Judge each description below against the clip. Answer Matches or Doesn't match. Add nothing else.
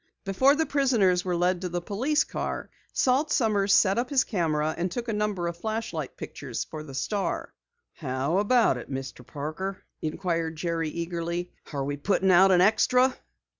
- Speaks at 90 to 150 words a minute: Doesn't match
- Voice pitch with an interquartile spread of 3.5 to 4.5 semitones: Doesn't match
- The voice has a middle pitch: Matches